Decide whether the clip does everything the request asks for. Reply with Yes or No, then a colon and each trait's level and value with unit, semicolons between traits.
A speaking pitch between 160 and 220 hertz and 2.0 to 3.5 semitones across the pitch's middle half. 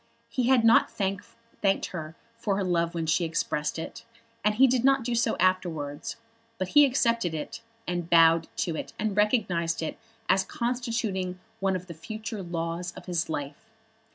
No: medium, 185 Hz; average, 5.3 semitones